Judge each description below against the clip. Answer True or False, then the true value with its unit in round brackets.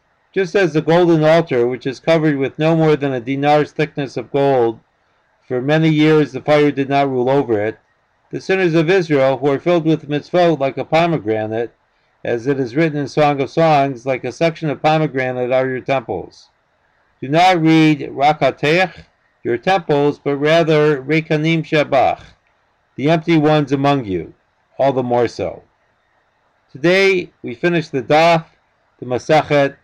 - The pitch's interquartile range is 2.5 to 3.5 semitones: True (3.2 semitones)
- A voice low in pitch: False (150 Hz)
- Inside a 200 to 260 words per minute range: False (165 wpm)